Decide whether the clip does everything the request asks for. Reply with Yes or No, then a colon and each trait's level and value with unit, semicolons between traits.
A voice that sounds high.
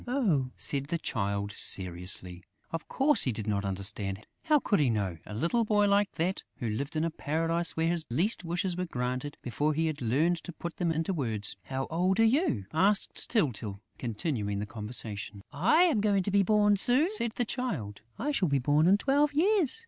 No: medium, 160 Hz